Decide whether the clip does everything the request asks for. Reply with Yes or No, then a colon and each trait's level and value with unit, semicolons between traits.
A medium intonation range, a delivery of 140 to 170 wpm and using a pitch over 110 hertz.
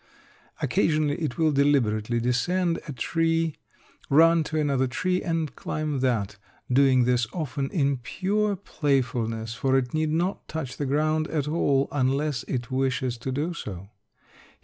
Yes: average, 4.0 semitones; average, 145 wpm; medium, 140 Hz